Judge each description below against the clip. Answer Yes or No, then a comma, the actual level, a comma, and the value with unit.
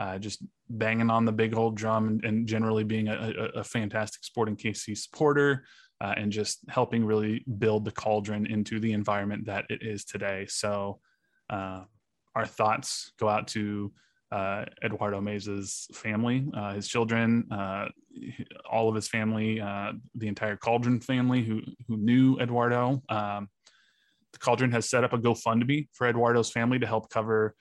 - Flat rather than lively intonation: Yes, narrow, 2.0 semitones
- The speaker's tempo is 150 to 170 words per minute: Yes, average, 165 wpm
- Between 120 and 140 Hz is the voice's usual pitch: No, low, 110 Hz